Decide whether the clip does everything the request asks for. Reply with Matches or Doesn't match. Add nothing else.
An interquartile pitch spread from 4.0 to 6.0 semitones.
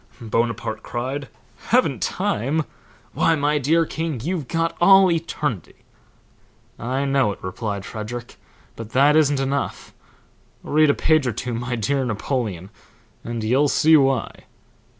Matches